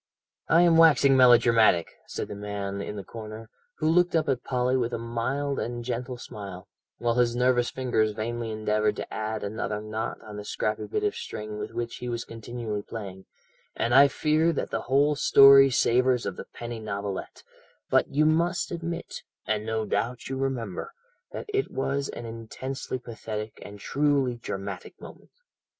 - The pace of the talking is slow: No, average, 170 wpm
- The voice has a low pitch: Yes, low, 120 Hz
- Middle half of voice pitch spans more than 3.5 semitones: Yes, average, 3.9 semitones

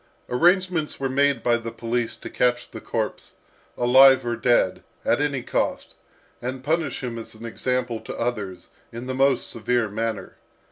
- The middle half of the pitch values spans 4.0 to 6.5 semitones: No, narrow, 2.6 semitones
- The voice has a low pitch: Yes, low, 125 Hz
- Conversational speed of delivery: Yes, average, 160 wpm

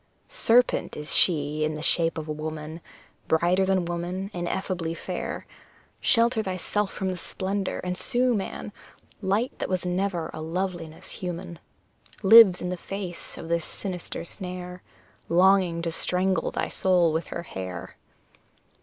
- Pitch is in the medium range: Yes, medium, 180 Hz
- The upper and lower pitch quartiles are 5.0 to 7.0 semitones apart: No, narrow, 2.4 semitones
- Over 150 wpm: No, average, 145 wpm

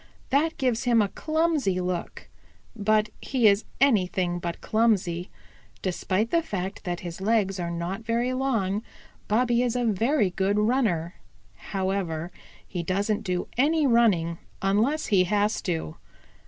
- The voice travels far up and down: No, average, 4.6 semitones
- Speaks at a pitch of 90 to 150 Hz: No, high, 205 Hz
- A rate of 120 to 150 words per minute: Yes, average, 140 wpm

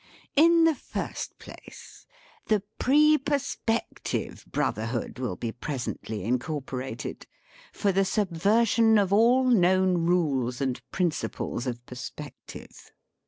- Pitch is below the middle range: No, medium, 180 Hz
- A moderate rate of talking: No, slow, 115 wpm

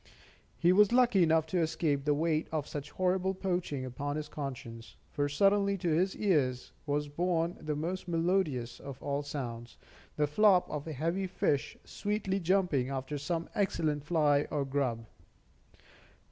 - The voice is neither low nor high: Yes, medium, 155 Hz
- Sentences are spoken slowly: No, average, 155 wpm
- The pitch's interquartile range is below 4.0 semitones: No, average, 4.3 semitones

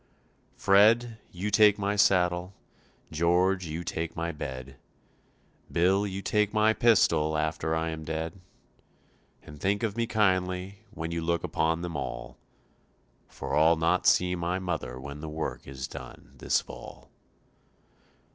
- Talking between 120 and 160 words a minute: Yes, slow, 135 wpm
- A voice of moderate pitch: No, very low, 85 Hz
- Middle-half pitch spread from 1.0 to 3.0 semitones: No, average, 3.7 semitones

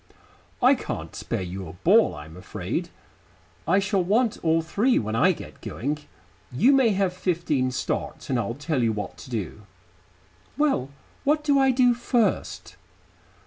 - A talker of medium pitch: Yes, medium, 165 Hz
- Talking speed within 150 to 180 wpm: Yes, average, 155 wpm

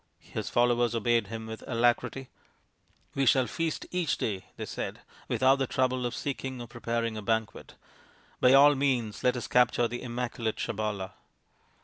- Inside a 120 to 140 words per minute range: No, average, 165 wpm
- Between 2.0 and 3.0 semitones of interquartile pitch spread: Yes, narrow, 2.5 semitones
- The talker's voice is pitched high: No, low, 120 Hz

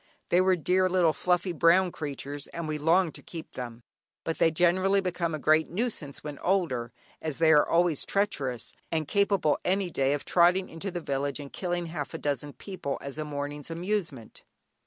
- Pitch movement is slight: No, average, 3.9 semitones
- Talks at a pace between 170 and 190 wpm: Yes, average, 185 wpm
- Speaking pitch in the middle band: Yes, medium, 165 Hz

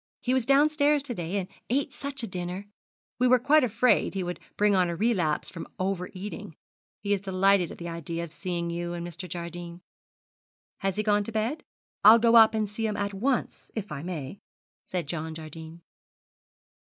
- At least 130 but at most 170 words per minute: No, average, 190 wpm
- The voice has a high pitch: Yes, high, 195 Hz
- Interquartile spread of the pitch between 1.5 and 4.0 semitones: No, average, 4.9 semitones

